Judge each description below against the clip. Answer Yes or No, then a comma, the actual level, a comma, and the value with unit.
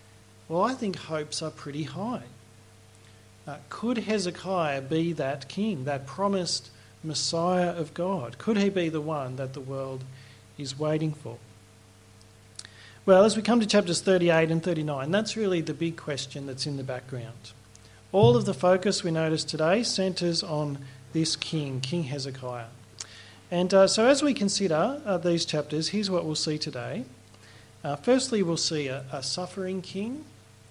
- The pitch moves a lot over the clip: Yes, wide, 6.7 semitones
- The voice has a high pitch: No, medium, 155 Hz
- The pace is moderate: Yes, average, 160 wpm